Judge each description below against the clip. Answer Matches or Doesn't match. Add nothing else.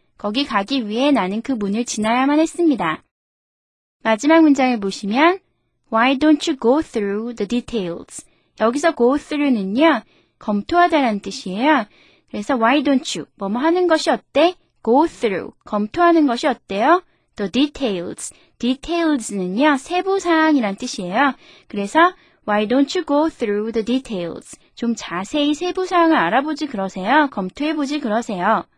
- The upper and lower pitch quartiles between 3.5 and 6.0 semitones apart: Doesn't match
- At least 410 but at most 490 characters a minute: Matches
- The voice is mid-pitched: Doesn't match